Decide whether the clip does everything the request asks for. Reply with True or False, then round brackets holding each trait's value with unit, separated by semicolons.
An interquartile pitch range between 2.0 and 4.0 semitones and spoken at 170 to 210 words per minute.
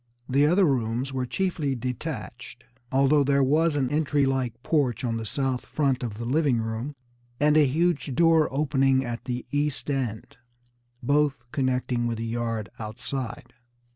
False (3.4 semitones; 155 wpm)